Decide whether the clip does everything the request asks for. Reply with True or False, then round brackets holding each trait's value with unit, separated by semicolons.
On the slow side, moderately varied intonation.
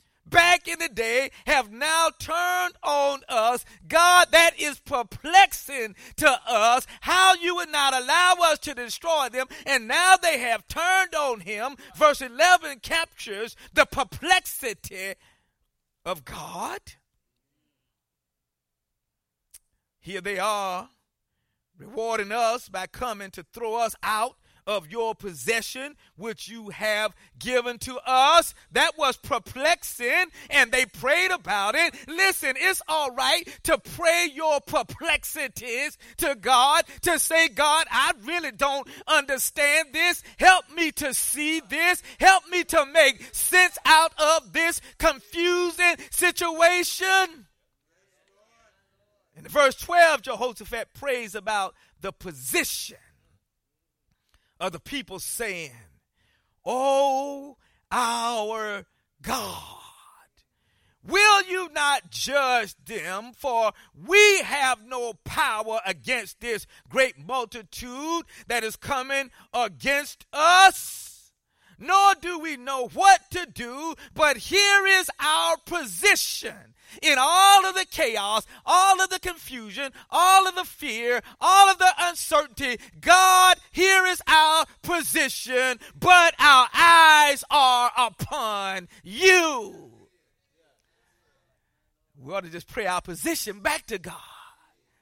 False (115 wpm; 6.9 semitones)